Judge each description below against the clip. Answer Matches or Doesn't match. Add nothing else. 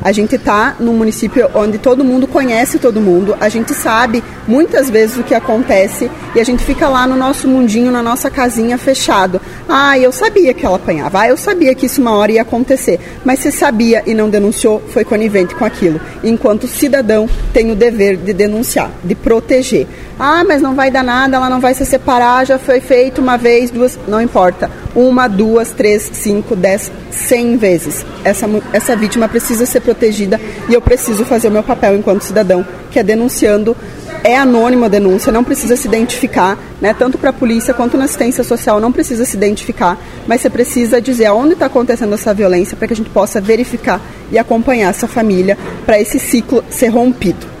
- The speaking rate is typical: Doesn't match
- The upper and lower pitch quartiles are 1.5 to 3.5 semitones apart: Matches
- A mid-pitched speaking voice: Doesn't match